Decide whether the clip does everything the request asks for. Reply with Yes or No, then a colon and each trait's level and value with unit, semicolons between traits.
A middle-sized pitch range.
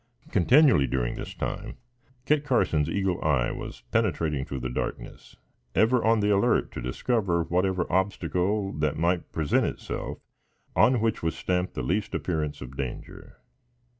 No: wide, 5.8 semitones